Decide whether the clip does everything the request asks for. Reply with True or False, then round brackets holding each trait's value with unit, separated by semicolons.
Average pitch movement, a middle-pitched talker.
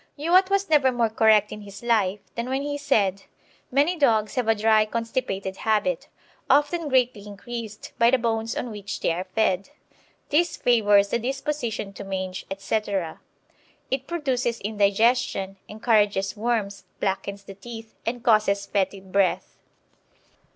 False (3.9 semitones; 220 Hz)